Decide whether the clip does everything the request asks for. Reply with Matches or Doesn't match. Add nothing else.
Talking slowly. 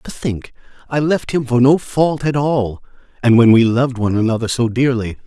Doesn't match